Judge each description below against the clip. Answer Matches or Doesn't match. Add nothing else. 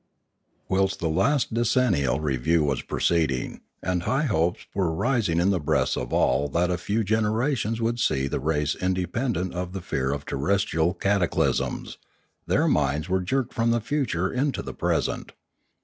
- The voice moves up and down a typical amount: Doesn't match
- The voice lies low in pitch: Matches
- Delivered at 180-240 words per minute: Doesn't match